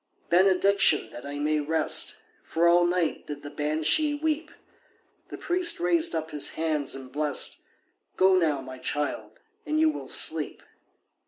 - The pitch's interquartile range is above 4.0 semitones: Yes, average, 4.5 semitones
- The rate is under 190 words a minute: Yes, average, 150 wpm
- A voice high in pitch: No, medium, 160 Hz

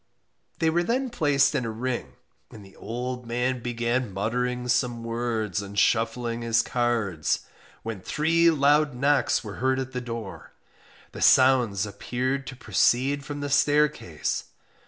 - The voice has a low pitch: Yes, low, 125 Hz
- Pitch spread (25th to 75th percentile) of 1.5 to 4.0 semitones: Yes, average, 3.1 semitones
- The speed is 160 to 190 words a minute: No, average, 145 wpm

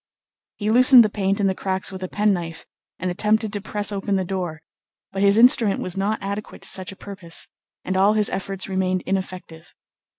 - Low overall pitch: No, high, 195 Hz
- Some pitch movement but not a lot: No, narrow, 1.9 semitones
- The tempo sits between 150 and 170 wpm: No, average, 195 wpm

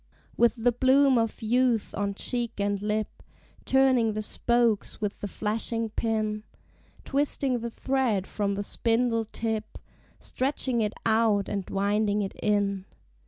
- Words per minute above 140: No, slow, 135 wpm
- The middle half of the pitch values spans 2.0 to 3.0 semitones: Yes, average, 2.7 semitones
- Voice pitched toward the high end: Yes, high, 225 Hz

